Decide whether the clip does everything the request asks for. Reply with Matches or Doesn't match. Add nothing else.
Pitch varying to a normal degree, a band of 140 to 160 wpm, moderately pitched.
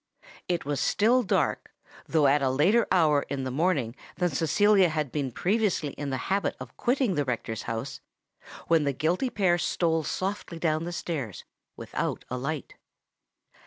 Matches